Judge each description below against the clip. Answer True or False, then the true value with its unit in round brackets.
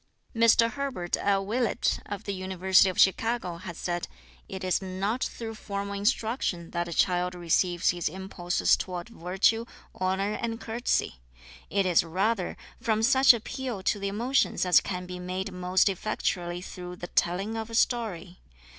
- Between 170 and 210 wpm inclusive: False (155 wpm)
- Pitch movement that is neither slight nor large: True (3.8 semitones)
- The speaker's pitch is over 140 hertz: True (190 Hz)